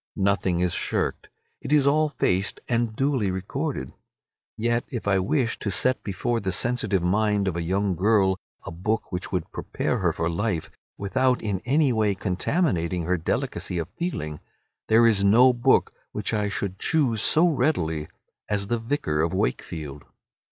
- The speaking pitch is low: Yes, low, 100 Hz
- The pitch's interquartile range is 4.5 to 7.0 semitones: Yes, average, 4.9 semitones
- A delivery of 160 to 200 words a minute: Yes, average, 165 wpm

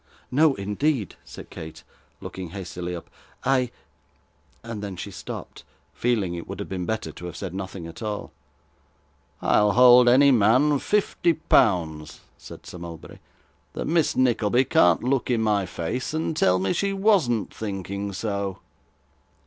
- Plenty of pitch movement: Yes, wide, 5.7 semitones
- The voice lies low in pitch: Yes, low, 105 Hz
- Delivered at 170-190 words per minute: No, average, 150 wpm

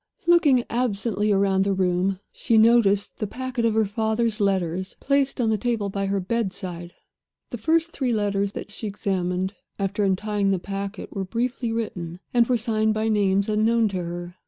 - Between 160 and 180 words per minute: Yes, average, 175 wpm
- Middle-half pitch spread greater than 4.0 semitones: No, average, 3.1 semitones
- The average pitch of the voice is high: Yes, high, 210 Hz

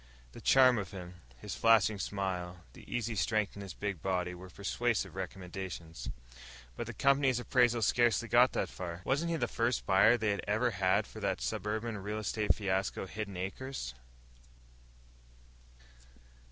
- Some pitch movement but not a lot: Yes, average, 4.1 semitones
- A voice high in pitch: No, low, 105 Hz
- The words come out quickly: No, average, 155 wpm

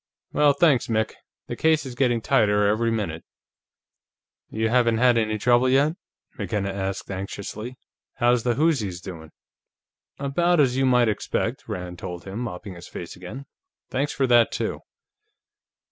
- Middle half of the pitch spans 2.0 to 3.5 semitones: No, average, 4.7 semitones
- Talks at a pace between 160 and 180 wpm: No, average, 145 wpm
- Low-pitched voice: Yes, low, 115 Hz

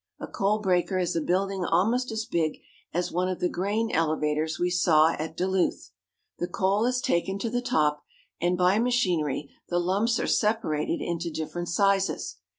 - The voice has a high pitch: No, medium, 180 Hz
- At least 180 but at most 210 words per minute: No, average, 170 wpm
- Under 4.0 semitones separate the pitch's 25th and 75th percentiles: Yes, average, 3.5 semitones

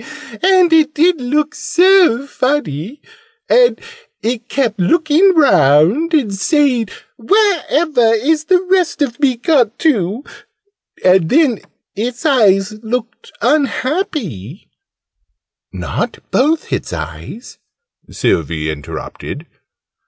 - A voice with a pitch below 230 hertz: No, very high, 275 Hz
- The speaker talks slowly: Yes, slow, 100 wpm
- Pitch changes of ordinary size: No, wide, 6.6 semitones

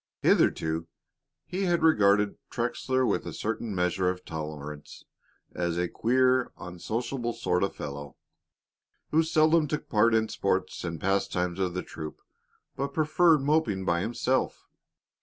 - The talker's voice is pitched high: No, low, 105 Hz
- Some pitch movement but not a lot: No, wide, 6.8 semitones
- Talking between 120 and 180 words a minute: Yes, average, 140 wpm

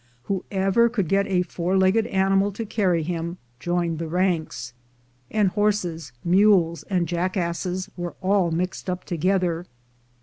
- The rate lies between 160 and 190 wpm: No, slow, 135 wpm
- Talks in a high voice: No, medium, 180 Hz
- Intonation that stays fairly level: Yes, narrow, 2.3 semitones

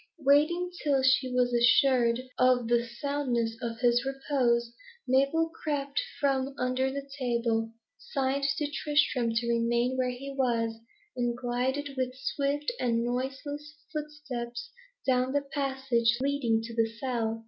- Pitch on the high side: Yes, very high, 255 Hz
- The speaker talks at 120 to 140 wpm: Yes, slow, 135 wpm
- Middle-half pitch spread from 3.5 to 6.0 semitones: No, average, 2.8 semitones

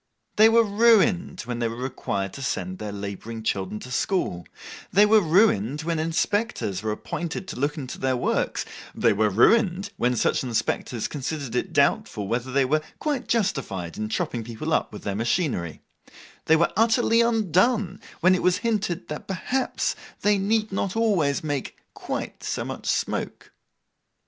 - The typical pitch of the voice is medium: Yes, medium, 155 Hz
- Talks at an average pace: Yes, average, 160 wpm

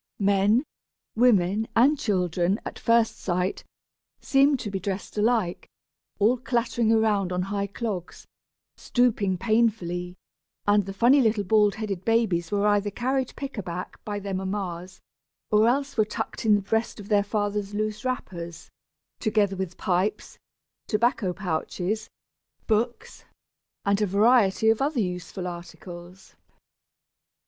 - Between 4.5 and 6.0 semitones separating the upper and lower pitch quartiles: No, average, 3.2 semitones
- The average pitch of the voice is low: No, high, 205 Hz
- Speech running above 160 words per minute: No, slow, 135 wpm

